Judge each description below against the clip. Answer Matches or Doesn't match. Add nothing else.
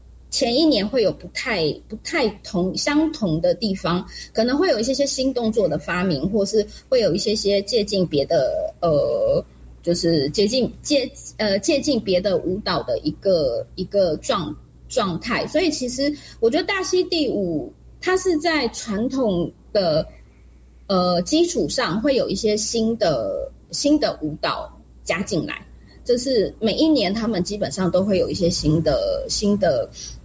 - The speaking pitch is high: Matches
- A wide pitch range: Matches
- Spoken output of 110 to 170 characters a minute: Doesn't match